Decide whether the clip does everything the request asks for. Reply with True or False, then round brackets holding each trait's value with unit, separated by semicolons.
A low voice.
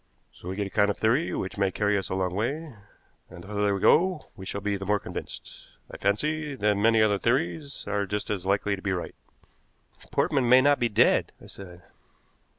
True (105 Hz)